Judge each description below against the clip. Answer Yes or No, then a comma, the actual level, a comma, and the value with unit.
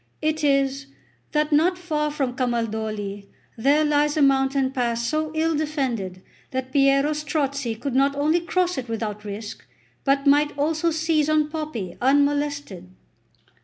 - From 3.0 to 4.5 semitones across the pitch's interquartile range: Yes, average, 3.7 semitones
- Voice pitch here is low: No, very high, 280 Hz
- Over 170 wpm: No, average, 140 wpm